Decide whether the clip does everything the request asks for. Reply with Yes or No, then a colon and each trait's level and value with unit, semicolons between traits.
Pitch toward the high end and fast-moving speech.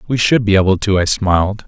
No: low, 100 Hz; fast, 250 wpm